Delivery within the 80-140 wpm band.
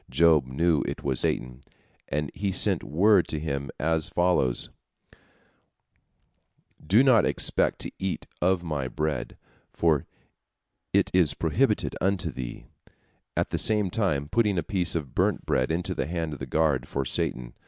No: average, 155 wpm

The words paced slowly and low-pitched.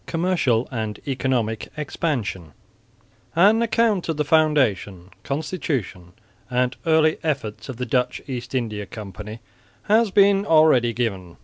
Yes: slow, 120 wpm; low, 125 Hz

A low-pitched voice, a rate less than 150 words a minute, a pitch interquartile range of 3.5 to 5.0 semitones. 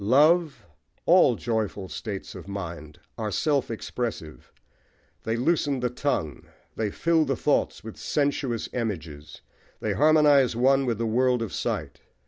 No: low, 120 Hz; slow, 135 wpm; wide, 5.4 semitones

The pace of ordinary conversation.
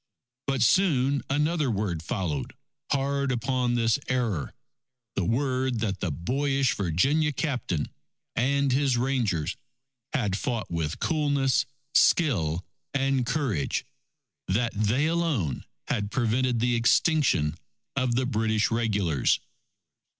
No: slow, 110 wpm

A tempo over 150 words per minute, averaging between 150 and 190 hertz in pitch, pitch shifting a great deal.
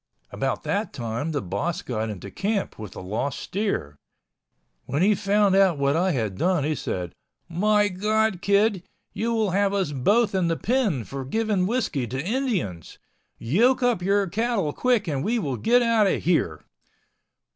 Yes: average, 170 wpm; medium, 185 Hz; wide, 7.8 semitones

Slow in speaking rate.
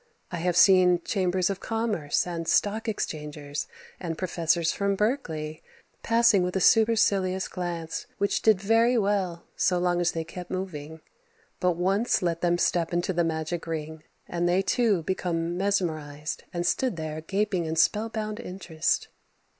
No: average, 150 wpm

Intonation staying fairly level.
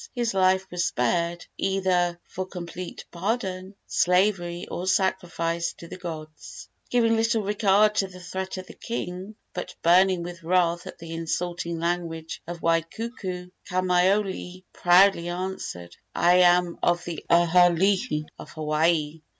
Yes: narrow, 1.9 semitones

